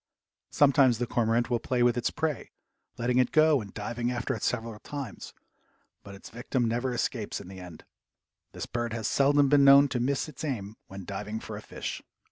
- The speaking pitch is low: Yes, low, 120 Hz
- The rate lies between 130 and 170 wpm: No, average, 195 wpm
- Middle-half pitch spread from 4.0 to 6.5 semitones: No, average, 3.4 semitones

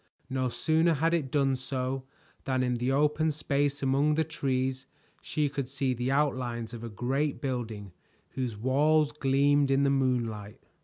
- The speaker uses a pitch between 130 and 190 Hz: Yes, low, 135 Hz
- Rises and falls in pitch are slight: Yes, narrow, 2.3 semitones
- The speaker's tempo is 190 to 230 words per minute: No, average, 160 wpm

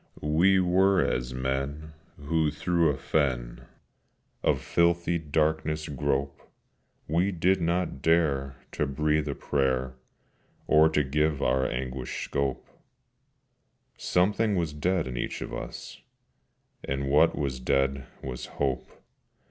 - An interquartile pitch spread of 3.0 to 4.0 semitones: Yes, average, 3.6 semitones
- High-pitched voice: No, very low, 75 Hz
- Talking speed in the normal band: No, slow, 120 wpm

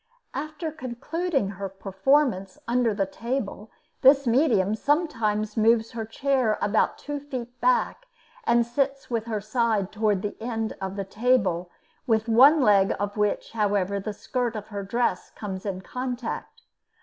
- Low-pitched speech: No, high, 225 Hz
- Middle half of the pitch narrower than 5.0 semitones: Yes, average, 4.1 semitones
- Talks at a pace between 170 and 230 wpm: No, average, 150 wpm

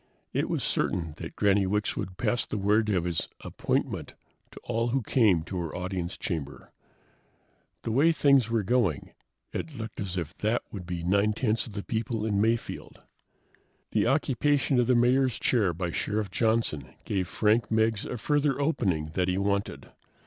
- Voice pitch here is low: Yes, low, 105 Hz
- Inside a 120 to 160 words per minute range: No, average, 170 wpm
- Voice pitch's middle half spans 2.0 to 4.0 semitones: No, average, 4.5 semitones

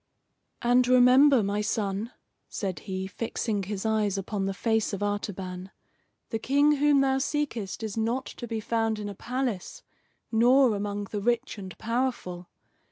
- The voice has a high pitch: Yes, high, 220 Hz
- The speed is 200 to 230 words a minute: No, average, 155 wpm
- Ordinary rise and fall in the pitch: Yes, average, 3.8 semitones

